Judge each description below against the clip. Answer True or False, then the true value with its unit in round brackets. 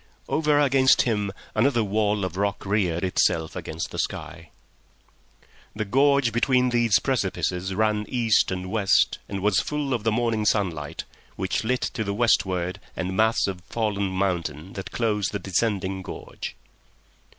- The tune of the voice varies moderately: True (3.7 semitones)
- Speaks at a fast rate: False (150 wpm)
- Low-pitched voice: True (105 Hz)